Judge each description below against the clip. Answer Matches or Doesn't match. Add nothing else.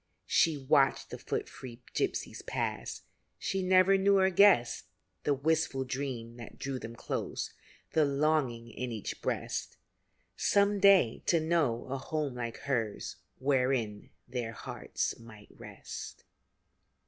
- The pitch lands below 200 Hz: Matches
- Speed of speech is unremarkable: Doesn't match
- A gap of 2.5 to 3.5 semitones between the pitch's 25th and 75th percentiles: Doesn't match